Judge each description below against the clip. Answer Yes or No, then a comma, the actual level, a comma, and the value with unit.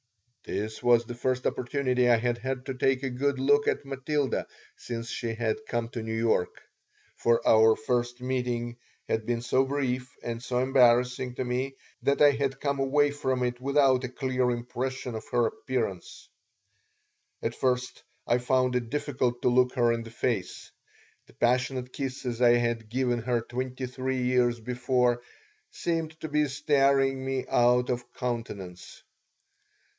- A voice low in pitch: Yes, low, 125 Hz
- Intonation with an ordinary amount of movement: No, narrow, 1.9 semitones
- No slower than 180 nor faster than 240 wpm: No, average, 160 wpm